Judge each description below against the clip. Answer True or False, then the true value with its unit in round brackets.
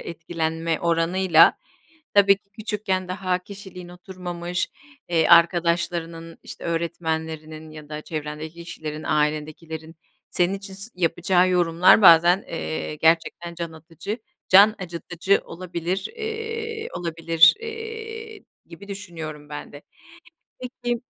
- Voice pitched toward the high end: False (175 Hz)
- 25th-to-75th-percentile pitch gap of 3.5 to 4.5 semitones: False (3.1 semitones)